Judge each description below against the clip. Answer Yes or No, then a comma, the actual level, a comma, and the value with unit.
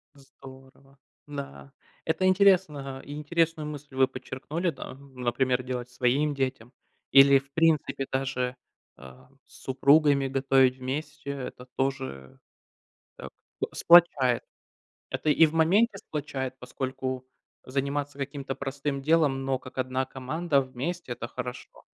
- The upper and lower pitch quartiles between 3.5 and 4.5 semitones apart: No, narrow, 2.4 semitones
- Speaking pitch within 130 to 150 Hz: Yes, low, 135 Hz